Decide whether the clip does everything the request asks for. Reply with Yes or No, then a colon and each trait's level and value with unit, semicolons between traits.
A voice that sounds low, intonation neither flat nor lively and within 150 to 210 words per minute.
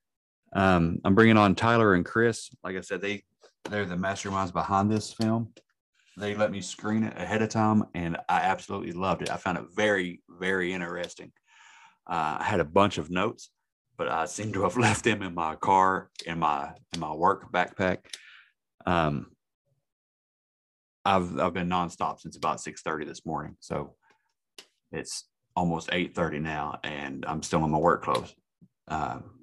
Yes: very low, 95 Hz; average, 3.3 semitones; average, 170 wpm